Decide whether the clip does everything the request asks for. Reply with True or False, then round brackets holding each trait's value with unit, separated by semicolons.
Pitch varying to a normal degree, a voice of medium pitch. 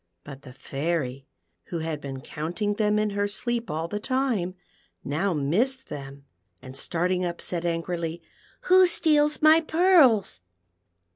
False (8.0 semitones; 180 Hz)